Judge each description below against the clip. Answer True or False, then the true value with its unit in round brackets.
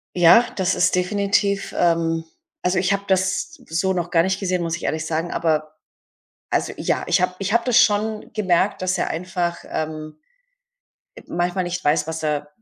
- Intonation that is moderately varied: True (3.0 semitones)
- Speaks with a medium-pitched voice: True (180 Hz)